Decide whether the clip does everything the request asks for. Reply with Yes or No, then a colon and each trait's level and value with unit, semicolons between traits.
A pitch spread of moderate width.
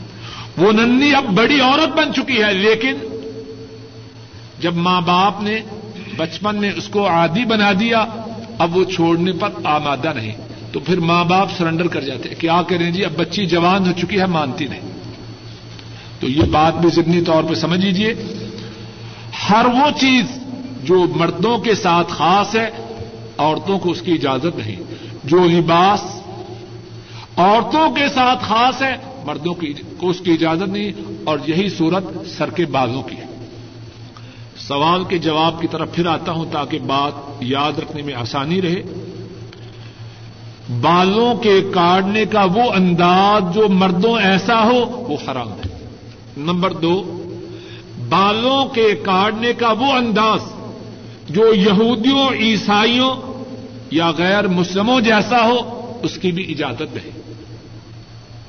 No: wide, 7.5 semitones